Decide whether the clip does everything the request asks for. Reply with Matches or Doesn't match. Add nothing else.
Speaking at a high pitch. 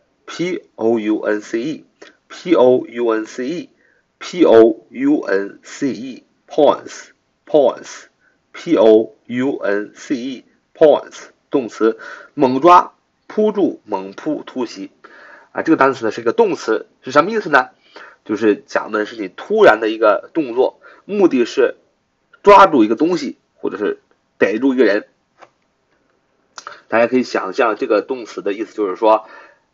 Matches